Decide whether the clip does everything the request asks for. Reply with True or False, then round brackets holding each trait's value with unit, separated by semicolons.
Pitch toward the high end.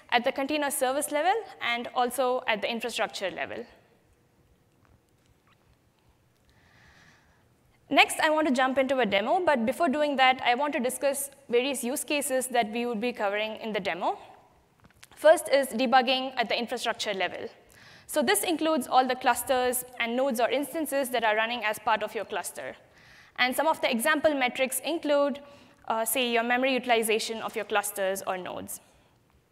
True (260 Hz)